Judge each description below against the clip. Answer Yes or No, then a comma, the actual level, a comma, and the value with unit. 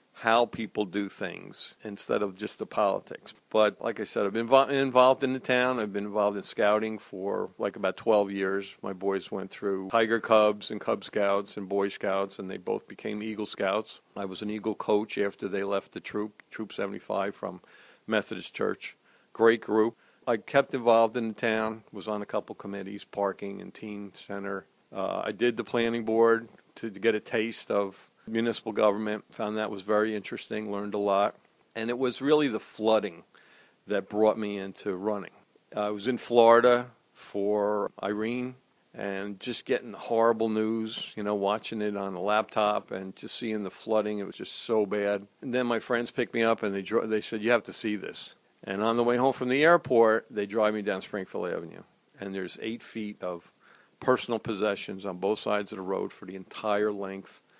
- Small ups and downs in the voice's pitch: Yes, narrow, 2.2 semitones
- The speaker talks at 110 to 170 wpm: No, average, 195 wpm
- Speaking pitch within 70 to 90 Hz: No, low, 105 Hz